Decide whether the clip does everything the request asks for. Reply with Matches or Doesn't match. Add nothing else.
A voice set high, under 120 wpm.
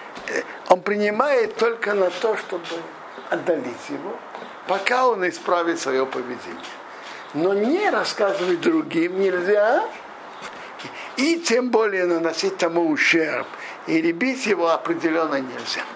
Matches